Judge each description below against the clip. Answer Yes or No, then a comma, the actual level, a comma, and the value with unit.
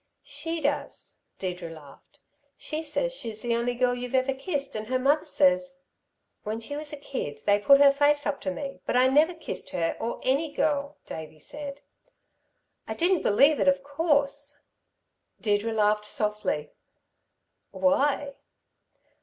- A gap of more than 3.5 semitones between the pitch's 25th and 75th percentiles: Yes, average, 4.7 semitones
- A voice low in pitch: No, very high, 275 Hz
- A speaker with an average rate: Yes, average, 155 wpm